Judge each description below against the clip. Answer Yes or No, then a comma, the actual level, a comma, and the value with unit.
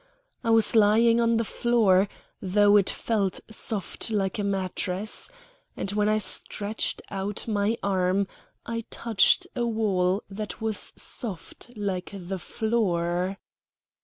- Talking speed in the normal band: No, slow, 130 wpm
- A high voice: Yes, high, 205 Hz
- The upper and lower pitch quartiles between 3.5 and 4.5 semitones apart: No, narrow, 2.6 semitones